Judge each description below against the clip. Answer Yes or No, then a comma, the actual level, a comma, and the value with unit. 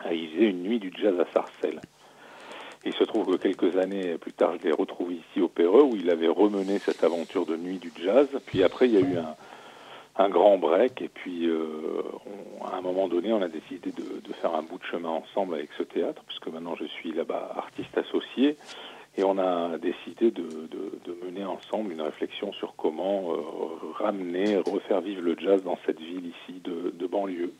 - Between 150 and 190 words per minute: No, average, 210 wpm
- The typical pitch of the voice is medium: No, low, 100 Hz